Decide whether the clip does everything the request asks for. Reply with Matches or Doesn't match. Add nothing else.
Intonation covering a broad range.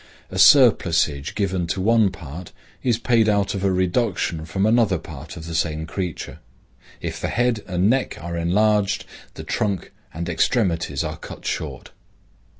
Doesn't match